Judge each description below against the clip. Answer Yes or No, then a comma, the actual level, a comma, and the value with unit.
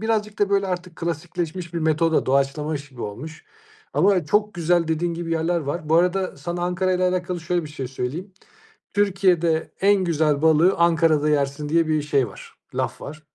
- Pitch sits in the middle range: Yes, medium, 165 Hz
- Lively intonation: No, average, 2.9 semitones